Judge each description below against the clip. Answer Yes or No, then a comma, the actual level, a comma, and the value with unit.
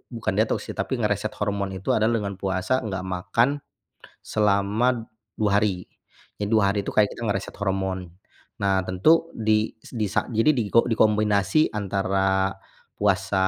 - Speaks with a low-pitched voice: Yes, low, 100 Hz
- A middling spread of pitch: No, narrow, 2.0 semitones